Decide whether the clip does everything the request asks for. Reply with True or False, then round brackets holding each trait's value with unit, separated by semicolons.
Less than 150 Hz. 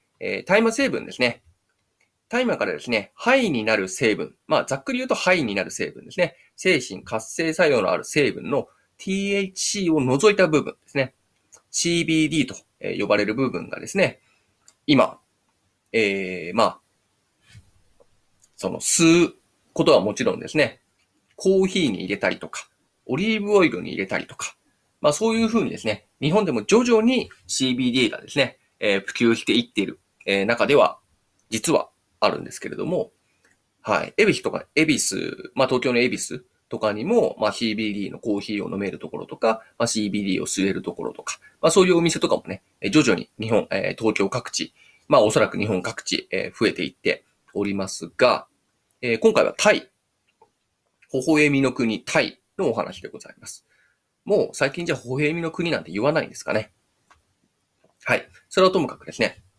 True (135 Hz)